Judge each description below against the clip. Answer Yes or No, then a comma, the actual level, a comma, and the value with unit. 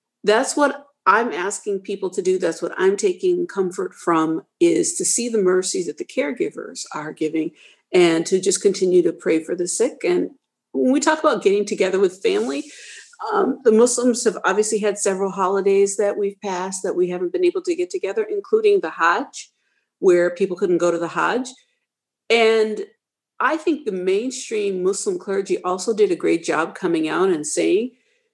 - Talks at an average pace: Yes, average, 180 wpm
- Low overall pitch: No, high, 220 Hz